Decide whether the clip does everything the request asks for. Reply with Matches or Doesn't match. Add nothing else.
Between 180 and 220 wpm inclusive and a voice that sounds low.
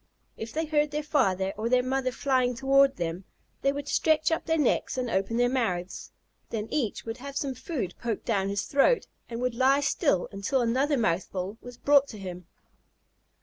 Doesn't match